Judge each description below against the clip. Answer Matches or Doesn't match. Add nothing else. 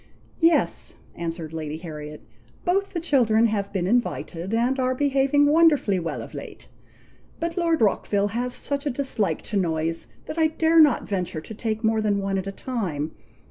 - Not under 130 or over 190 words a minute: Matches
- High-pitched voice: Matches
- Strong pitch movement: Matches